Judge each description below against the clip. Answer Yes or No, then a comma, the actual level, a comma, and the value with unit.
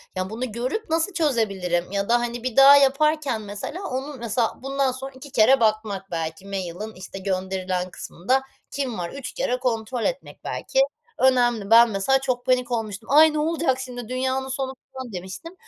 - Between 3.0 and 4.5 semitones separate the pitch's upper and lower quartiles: No, average, 5.1 semitones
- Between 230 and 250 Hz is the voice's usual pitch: Yes, high, 245 Hz